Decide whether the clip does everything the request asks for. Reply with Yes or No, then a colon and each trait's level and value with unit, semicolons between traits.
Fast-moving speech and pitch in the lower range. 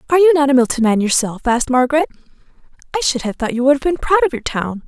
No: fast, 260 wpm; very high, 260 Hz